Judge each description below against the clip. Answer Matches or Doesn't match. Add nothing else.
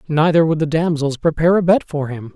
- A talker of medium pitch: Matches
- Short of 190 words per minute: Doesn't match